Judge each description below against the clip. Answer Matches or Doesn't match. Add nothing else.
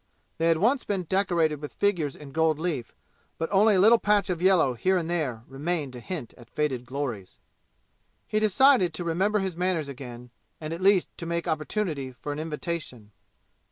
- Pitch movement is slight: Doesn't match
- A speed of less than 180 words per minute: Doesn't match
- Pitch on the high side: Doesn't match